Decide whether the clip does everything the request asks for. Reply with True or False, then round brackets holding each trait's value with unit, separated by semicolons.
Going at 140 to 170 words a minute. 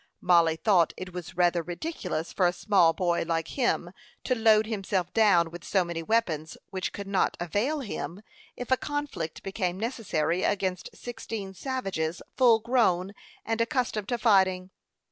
True (155 wpm)